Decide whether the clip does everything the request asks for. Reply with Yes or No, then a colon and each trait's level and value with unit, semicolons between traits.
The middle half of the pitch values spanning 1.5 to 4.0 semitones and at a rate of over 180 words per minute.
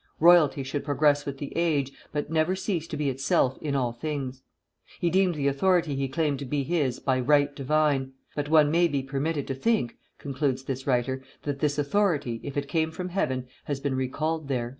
Yes: average, 2.8 semitones; average, 200 wpm